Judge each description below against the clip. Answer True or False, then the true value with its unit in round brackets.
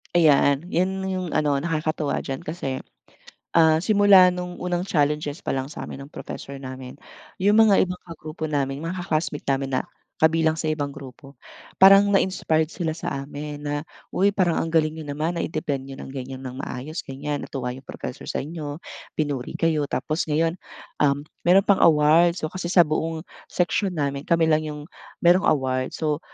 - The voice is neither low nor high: True (155 Hz)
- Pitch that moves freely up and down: False (3.4 semitones)